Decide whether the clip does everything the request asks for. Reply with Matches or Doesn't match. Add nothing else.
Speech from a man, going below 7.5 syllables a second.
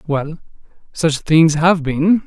Matches